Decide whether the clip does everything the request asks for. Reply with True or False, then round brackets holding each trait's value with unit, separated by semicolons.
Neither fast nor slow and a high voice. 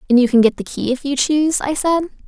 False (290 wpm; 275 Hz)